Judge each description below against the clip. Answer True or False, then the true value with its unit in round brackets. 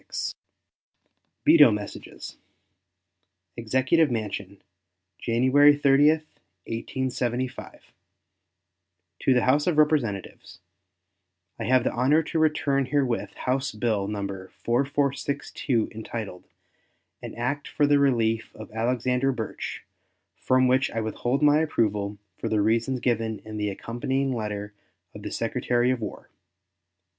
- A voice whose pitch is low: True (125 Hz)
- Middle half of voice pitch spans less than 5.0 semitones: True (4.0 semitones)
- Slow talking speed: True (115 wpm)